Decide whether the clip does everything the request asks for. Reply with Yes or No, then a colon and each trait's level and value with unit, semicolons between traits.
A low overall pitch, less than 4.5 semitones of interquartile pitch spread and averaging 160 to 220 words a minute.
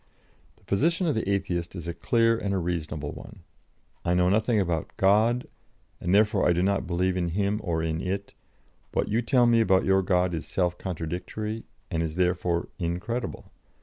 Yes: very low, 95 Hz; average, 3.6 semitones; average, 180 wpm